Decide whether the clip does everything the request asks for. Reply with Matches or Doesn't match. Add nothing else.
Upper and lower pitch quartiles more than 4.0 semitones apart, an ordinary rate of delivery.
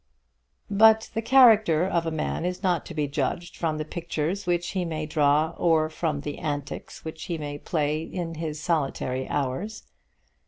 Doesn't match